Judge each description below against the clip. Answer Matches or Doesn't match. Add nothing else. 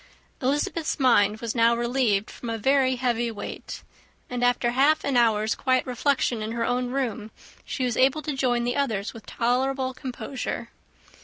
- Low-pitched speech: Doesn't match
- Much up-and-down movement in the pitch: Doesn't match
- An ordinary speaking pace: Matches